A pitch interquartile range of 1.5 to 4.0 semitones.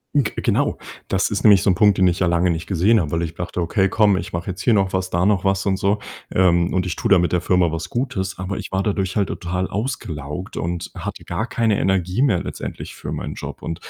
Yes: narrow, 2.4 semitones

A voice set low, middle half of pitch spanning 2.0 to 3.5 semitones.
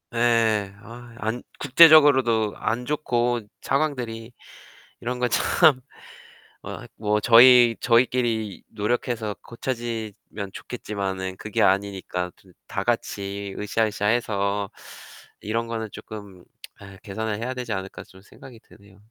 Yes: low, 110 Hz; average, 3.2 semitones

